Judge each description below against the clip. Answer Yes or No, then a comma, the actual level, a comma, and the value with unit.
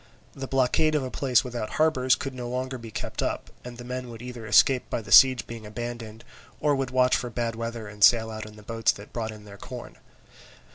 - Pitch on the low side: Yes, low, 120 Hz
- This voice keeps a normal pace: No, fast, 230 wpm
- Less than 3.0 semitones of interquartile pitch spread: Yes, narrow, 2.4 semitones